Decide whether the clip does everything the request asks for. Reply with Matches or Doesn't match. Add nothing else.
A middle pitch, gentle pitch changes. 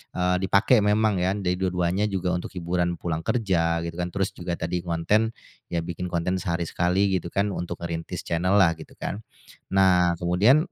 Doesn't match